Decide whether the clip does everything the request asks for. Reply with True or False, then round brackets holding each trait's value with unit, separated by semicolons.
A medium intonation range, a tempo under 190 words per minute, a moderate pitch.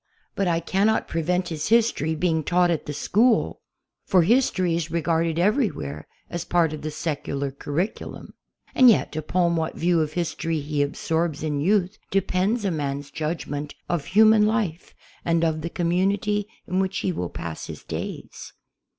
True (3.7 semitones; 160 wpm; 170 Hz)